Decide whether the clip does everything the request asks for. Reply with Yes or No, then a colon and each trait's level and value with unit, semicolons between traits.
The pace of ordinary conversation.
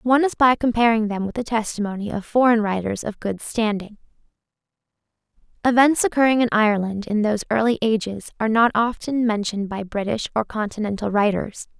Yes: average, 160 wpm